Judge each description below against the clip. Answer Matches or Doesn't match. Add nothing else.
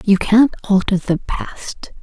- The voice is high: Matches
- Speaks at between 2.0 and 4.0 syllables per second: Matches